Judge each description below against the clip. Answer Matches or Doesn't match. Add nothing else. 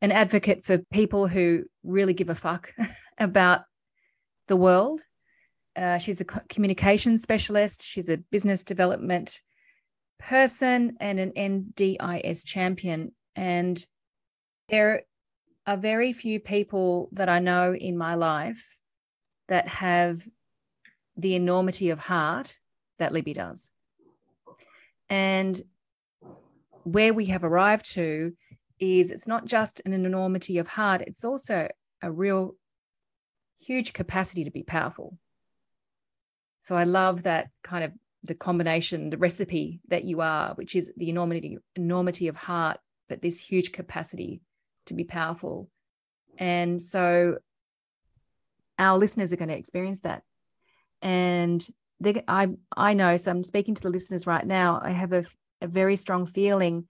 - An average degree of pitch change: Doesn't match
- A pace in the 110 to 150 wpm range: Matches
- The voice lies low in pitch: Doesn't match